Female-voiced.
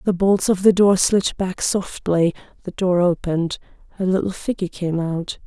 Yes: female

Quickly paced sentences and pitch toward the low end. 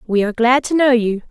No: fast, 275 wpm; high, 240 Hz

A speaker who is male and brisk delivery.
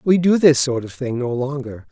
Yes: male; fast, 250 wpm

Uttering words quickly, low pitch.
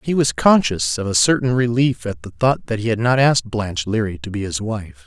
Yes: fast, 250 wpm; low, 110 Hz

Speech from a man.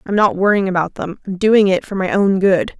No: female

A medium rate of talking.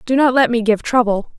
No: fast, 260 wpm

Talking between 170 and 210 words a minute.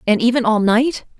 Yes: average, 200 wpm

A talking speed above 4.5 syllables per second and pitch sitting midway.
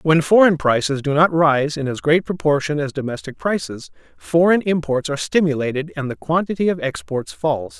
Yes: 5.2 syllables/s; medium, 150 Hz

